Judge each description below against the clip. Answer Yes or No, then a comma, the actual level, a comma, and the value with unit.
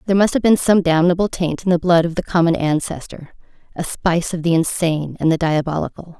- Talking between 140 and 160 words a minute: No, fast, 205 wpm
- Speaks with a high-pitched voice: No, medium, 170 Hz